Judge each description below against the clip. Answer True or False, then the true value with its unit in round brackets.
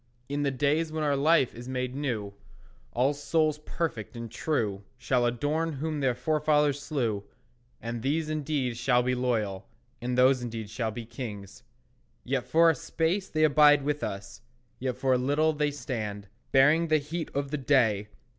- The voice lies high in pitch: False (135 Hz)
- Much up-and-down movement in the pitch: False (4.1 semitones)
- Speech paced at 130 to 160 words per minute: False (170 wpm)